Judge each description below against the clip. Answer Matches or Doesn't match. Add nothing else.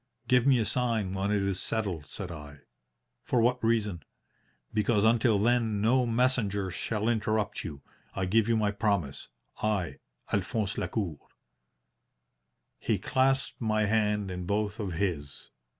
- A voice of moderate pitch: Doesn't match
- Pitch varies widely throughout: Doesn't match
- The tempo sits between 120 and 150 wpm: Matches